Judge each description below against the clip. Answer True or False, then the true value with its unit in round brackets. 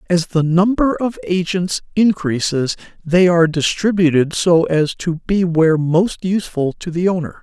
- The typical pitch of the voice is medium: True (170 Hz)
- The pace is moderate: True (155 wpm)